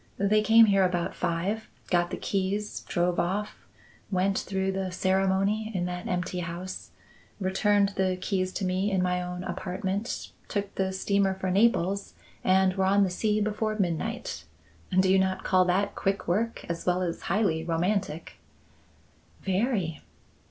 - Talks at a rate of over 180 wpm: No, average, 150 wpm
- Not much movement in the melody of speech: Yes, narrow, 1.8 semitones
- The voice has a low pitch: No, high, 190 Hz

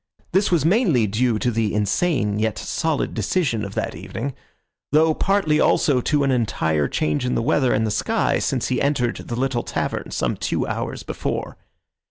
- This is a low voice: Yes, low, 125 Hz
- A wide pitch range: Yes, wide, 5.8 semitones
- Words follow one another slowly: No, average, 180 wpm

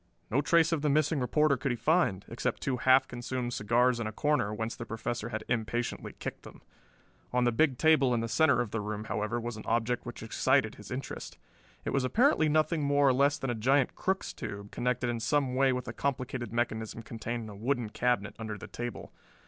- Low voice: Yes, low, 125 Hz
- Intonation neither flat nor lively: Yes, average, 3.6 semitones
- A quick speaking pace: Yes, fast, 215 wpm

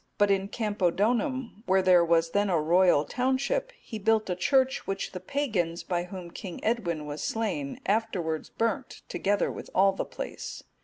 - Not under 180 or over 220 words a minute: No, average, 165 wpm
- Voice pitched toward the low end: No, high, 195 Hz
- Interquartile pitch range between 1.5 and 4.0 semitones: No, average, 4.5 semitones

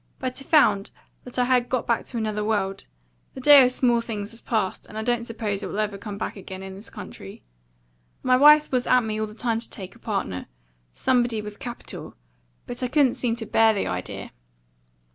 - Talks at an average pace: No, fast, 210 wpm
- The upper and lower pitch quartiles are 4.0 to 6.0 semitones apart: No, average, 3.1 semitones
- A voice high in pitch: Yes, high, 230 Hz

